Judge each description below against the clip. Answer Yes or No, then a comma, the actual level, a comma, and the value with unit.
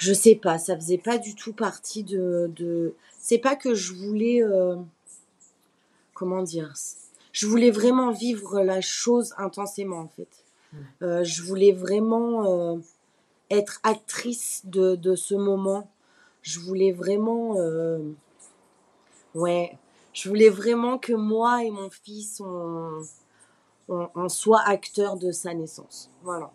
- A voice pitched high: Yes, high, 195 Hz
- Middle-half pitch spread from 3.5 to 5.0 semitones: Yes, average, 4.0 semitones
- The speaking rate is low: Yes, slow, 140 wpm